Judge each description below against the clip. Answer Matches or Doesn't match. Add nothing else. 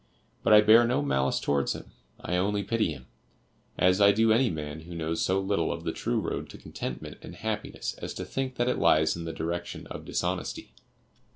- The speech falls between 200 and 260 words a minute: Matches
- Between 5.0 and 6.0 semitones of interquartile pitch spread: Matches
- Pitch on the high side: Doesn't match